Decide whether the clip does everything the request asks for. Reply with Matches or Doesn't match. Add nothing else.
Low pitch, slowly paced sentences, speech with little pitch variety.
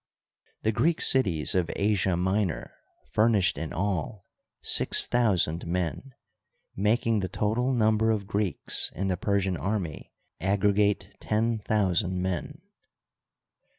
Doesn't match